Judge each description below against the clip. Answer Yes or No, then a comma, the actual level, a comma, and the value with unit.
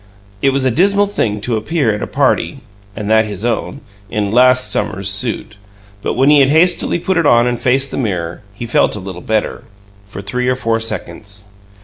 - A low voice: Yes, low, 120 Hz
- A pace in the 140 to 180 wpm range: No, fast, 205 wpm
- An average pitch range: Yes, average, 4.6 semitones